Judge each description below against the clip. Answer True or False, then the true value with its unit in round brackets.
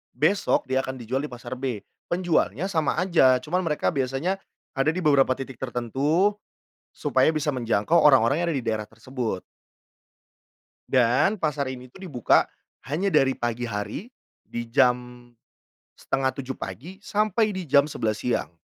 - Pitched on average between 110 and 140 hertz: True (135 Hz)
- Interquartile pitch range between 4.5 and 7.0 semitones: True (4.8 semitones)